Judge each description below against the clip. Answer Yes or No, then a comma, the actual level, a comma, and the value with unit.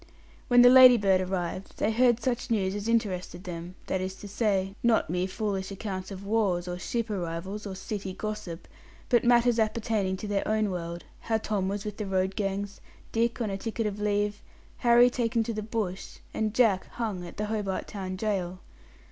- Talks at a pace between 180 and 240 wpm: Yes, average, 190 wpm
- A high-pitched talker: Yes, high, 205 Hz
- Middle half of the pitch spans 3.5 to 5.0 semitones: No, average, 3.0 semitones